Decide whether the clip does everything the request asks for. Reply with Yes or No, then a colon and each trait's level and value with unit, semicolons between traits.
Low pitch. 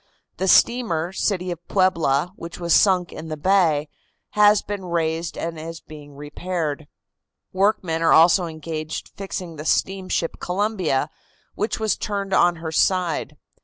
No: medium, 170 Hz